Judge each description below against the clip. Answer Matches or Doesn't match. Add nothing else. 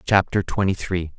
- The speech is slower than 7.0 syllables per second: Matches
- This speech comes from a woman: Doesn't match